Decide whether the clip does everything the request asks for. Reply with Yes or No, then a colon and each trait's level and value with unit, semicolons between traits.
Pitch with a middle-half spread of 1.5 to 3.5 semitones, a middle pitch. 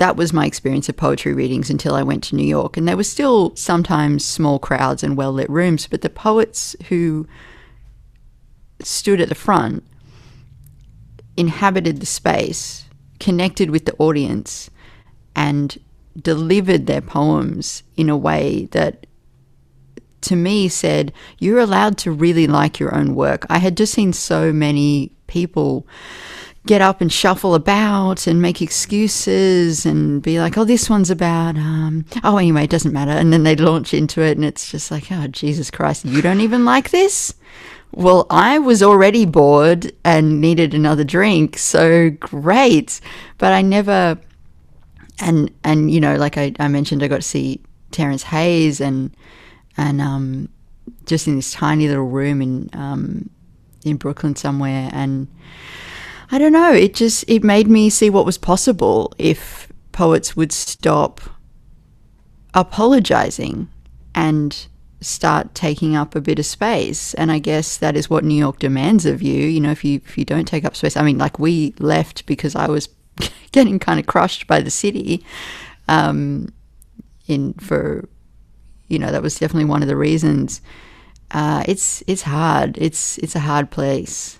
No: average, 4.2 semitones; medium, 155 Hz